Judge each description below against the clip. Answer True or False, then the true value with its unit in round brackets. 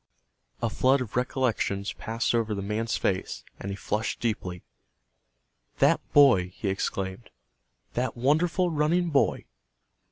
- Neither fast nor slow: False (125 wpm)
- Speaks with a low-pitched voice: True (115 Hz)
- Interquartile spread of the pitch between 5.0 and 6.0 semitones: True (5.6 semitones)